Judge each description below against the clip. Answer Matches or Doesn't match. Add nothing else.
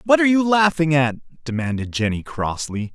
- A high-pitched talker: Doesn't match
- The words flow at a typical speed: Matches